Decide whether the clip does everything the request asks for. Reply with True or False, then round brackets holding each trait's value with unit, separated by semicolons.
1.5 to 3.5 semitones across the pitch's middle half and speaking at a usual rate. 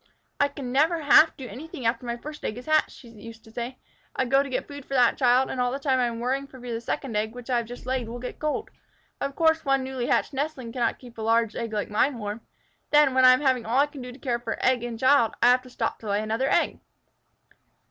False (2.8 semitones; 270 wpm)